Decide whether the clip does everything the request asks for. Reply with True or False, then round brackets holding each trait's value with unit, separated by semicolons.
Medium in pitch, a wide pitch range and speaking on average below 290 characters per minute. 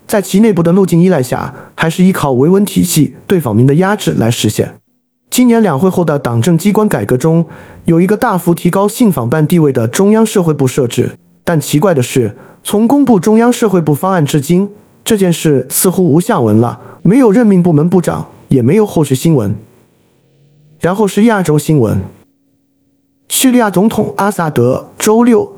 True (170 Hz; 6.7 semitones; 275 characters per minute)